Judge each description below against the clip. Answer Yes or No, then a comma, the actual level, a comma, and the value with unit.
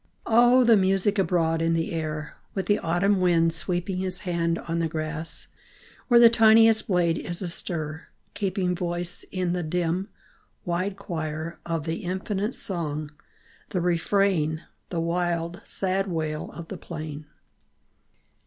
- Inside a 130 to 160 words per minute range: Yes, average, 140 wpm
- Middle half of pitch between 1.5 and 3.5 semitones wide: Yes, average, 2.8 semitones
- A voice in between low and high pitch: Yes, medium, 175 Hz